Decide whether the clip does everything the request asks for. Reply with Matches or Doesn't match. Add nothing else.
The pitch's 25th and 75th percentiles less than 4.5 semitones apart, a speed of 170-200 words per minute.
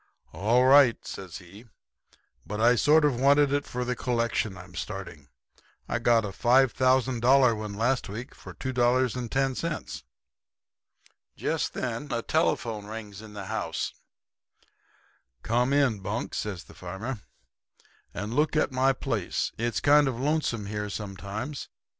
Doesn't match